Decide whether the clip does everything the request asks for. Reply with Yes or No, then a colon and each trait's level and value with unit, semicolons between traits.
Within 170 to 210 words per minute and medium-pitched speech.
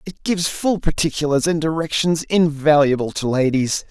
No: average, 140 wpm; medium, 155 Hz